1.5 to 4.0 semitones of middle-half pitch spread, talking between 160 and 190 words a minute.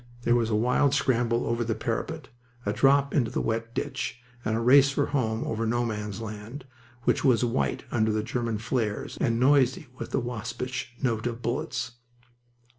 Yes: narrow, 2.4 semitones; average, 180 wpm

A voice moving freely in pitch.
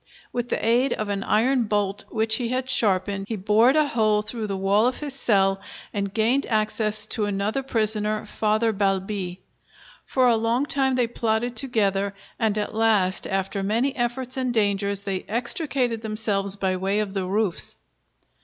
No: average, 3.2 semitones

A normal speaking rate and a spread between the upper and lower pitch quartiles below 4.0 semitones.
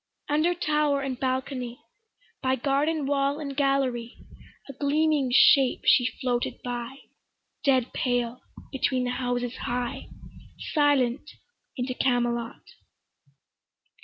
No: slow, 105 wpm; narrow, 2.4 semitones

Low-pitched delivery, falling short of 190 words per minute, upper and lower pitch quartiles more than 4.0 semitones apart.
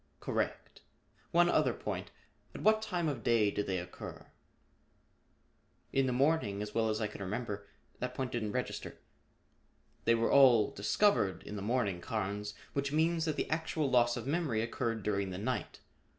Yes: low, 115 Hz; average, 165 wpm; average, 5.3 semitones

